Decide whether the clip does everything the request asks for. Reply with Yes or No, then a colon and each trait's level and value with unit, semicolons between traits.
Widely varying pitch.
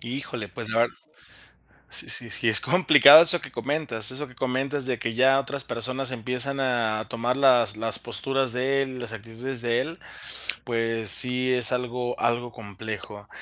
No: average, 2.7 semitones